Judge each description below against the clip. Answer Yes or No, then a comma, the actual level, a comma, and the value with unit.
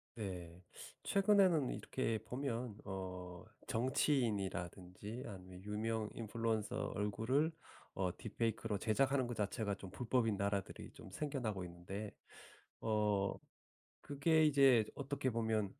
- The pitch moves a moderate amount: Yes, average, 4.8 semitones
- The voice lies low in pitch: Yes, low, 110 Hz